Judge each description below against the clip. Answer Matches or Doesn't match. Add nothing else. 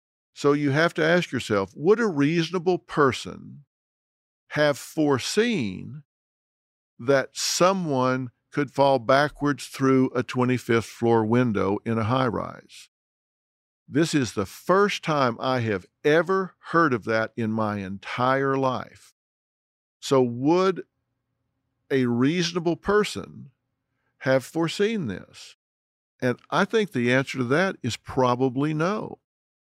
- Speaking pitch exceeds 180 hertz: Doesn't match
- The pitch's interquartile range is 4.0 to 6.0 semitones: Matches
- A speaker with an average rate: Doesn't match